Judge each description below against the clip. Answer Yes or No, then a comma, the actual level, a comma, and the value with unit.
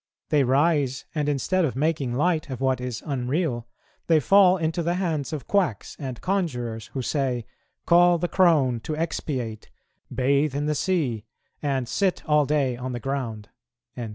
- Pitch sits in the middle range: Yes, medium, 145 Hz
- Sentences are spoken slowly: No, average, 160 wpm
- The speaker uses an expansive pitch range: No, average, 4.6 semitones